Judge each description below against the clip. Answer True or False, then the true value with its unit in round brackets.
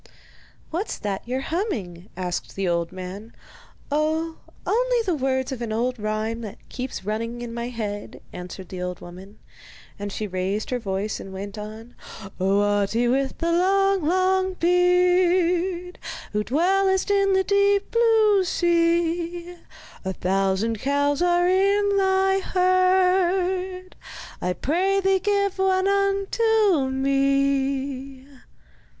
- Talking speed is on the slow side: True (130 wpm)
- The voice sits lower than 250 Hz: False (310 Hz)